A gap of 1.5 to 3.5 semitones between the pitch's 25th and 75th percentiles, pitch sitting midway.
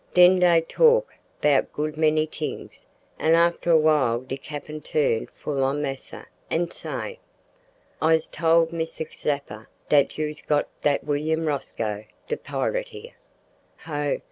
Yes: narrow, 2.5 semitones; medium, 155 Hz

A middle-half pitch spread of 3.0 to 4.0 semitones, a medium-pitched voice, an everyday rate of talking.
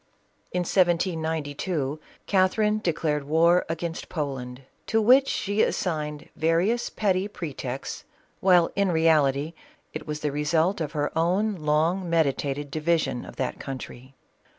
No: average, 3.7 semitones; medium, 160 Hz; slow, 130 wpm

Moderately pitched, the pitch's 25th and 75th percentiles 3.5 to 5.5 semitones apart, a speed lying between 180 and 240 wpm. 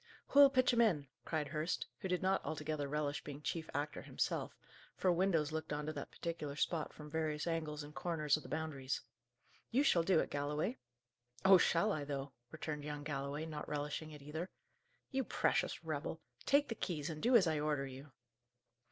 No: medium, 155 Hz; narrow, 2.6 semitones; average, 185 wpm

